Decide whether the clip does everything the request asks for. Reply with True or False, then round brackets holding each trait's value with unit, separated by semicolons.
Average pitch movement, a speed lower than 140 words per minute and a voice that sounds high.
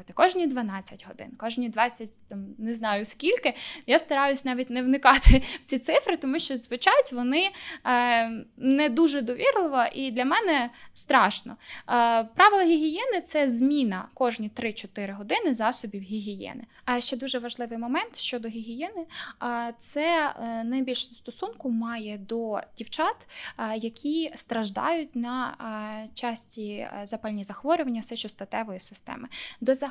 True (4.3 semitones; 120 wpm; 245 Hz)